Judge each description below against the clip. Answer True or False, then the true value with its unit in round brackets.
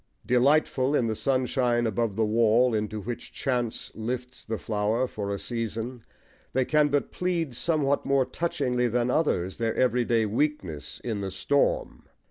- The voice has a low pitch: True (120 Hz)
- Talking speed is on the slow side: False (150 wpm)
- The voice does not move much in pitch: False (3.2 semitones)